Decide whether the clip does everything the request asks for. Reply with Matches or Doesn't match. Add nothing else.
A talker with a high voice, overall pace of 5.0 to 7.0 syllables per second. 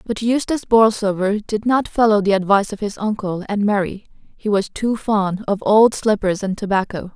Matches